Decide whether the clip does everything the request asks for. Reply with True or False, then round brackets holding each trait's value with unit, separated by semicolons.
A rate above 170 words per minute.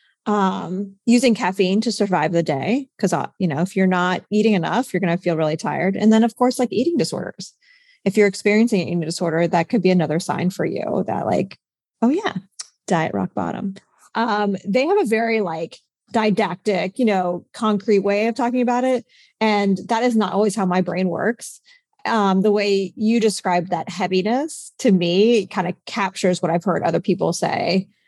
True (190 wpm)